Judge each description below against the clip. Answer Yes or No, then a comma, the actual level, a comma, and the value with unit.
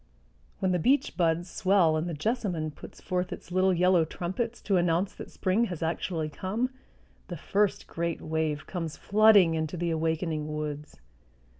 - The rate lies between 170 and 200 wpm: No, average, 160 wpm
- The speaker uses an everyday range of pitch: Yes, average, 3.0 semitones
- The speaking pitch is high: No, medium, 175 Hz